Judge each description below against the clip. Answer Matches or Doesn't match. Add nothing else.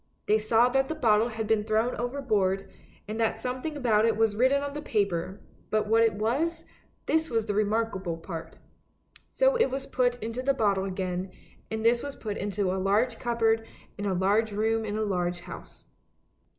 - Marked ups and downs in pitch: Doesn't match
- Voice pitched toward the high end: Matches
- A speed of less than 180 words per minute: Doesn't match